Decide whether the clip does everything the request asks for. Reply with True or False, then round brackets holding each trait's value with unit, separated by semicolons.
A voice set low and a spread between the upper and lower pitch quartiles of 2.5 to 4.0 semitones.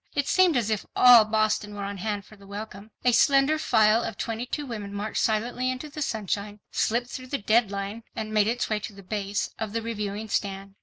False (215 Hz; 2.9 semitones)